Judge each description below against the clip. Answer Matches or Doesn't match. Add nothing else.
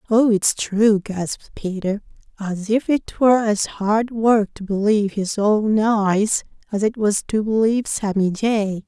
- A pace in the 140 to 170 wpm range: Matches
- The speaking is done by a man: Doesn't match